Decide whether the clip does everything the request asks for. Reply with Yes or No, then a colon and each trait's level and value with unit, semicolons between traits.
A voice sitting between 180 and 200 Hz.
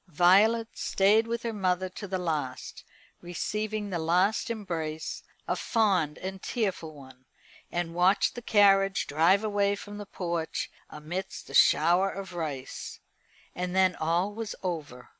Yes: medium, 185 Hz